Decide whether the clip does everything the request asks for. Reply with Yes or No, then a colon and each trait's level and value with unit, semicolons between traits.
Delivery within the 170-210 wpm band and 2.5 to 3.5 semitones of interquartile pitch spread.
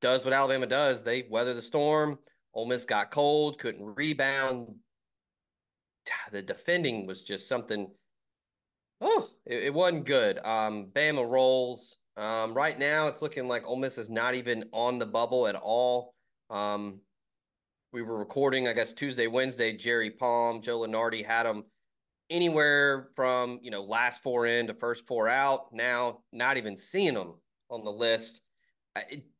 No: average, 155 wpm; average, 3.1 semitones